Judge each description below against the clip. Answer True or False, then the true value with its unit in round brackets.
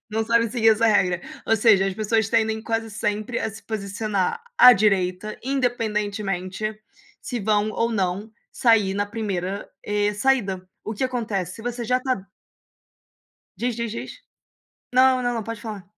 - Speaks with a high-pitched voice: True (215 Hz)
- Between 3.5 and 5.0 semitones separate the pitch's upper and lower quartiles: False (2.5 semitones)